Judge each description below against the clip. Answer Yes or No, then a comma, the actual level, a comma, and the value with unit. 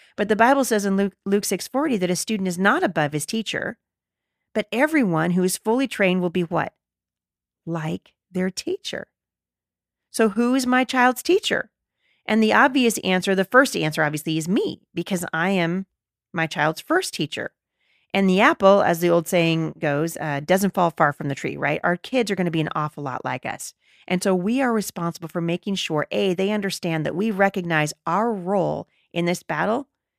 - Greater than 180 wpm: Yes, average, 190 wpm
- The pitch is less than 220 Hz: Yes, medium, 185 Hz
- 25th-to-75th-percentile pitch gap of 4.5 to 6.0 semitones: Yes, average, 4.9 semitones